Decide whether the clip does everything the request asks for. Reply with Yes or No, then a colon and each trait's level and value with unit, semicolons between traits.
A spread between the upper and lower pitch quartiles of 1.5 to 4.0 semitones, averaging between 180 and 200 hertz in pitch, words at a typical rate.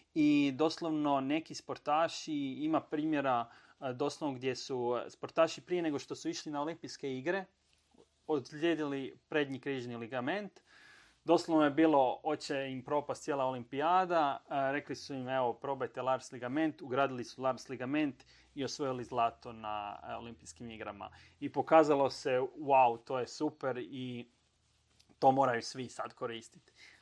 No: average, 3.7 semitones; medium, 140 Hz; average, 135 wpm